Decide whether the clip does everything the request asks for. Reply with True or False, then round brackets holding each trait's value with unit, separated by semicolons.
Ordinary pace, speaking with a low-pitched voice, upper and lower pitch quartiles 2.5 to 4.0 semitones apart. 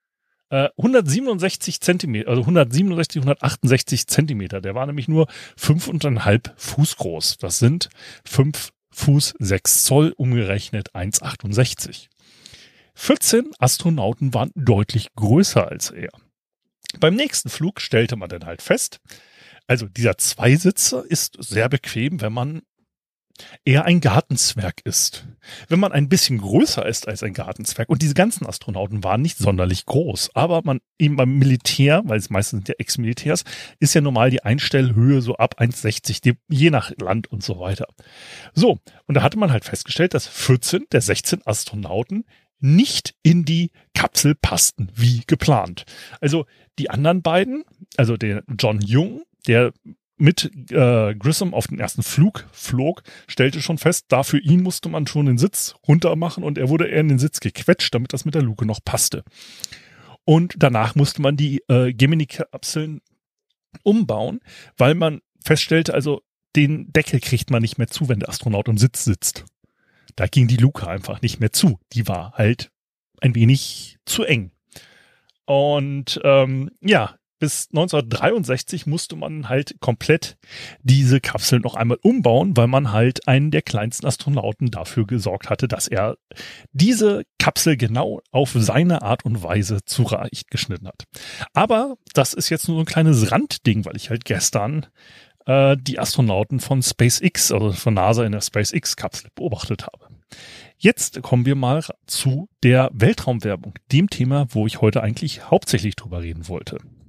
False (150 wpm; 130 Hz; 5.3 semitones)